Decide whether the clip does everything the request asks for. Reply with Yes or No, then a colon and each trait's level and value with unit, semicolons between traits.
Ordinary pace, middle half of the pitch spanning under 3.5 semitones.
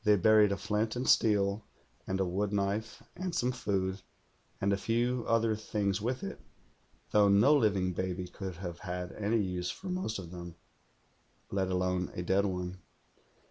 Yes: average, 165 wpm; average, 2.9 semitones